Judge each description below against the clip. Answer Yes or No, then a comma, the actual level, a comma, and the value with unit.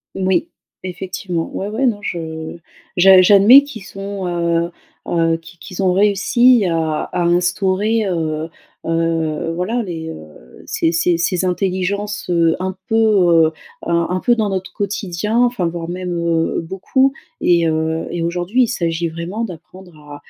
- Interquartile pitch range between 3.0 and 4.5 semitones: Yes, average, 3.3 semitones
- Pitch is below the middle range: No, medium, 180 Hz